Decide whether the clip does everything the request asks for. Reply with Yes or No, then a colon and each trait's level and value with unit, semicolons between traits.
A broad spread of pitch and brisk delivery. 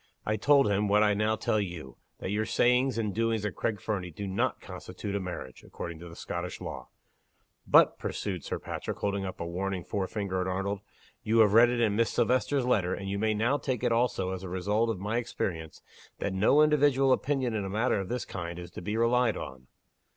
No: average, 3.7 semitones; fast, 215 wpm